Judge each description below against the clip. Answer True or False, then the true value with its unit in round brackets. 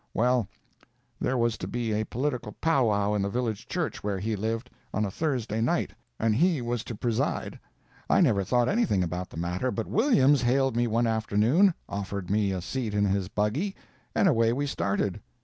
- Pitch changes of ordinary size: True (3.8 semitones)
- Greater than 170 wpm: True (190 wpm)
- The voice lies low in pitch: True (115 Hz)